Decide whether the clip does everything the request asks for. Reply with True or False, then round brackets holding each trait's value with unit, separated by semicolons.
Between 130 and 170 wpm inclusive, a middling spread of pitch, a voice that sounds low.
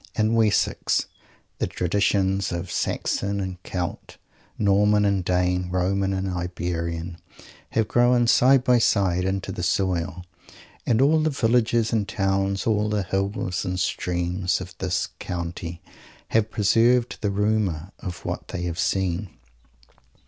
True (135 wpm; 3.0 semitones; 95 Hz)